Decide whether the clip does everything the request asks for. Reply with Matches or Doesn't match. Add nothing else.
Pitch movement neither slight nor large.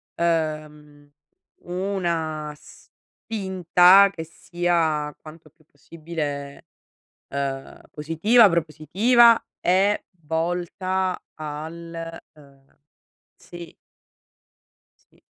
Matches